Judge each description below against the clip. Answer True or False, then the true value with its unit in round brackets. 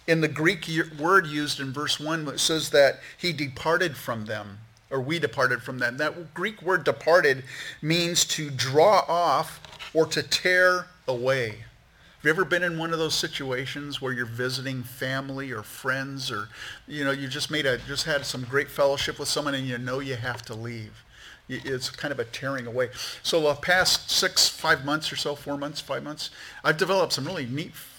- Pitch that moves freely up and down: False (3.7 semitones)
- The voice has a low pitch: False (145 Hz)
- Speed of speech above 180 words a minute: True (195 wpm)